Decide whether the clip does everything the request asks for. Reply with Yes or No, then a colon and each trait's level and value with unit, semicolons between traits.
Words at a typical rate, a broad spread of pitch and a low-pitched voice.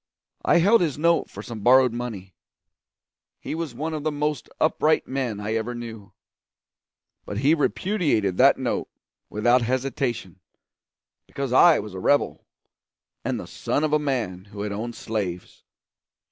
Yes: average, 150 wpm; wide, 5.9 semitones; low, 125 Hz